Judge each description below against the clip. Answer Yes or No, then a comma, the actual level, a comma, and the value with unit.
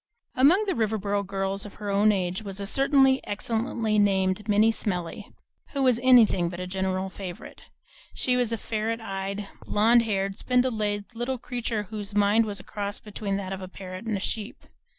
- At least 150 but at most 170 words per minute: No, average, 185 wpm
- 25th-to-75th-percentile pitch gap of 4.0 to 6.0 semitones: No, average, 2.7 semitones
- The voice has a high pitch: Yes, high, 210 Hz